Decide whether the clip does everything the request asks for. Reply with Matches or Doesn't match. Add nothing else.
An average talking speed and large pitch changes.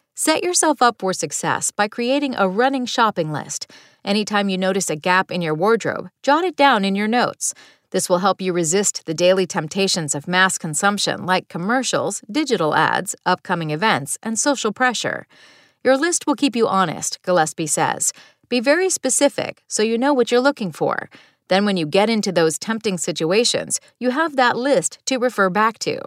Matches